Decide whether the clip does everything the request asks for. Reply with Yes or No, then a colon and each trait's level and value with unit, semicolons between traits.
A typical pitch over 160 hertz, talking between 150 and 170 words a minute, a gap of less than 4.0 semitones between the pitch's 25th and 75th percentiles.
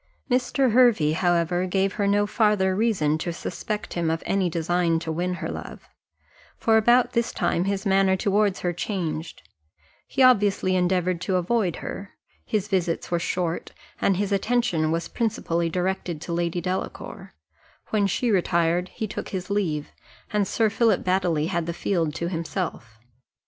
Yes: medium, 185 Hz; average, 160 wpm; average, 3.3 semitones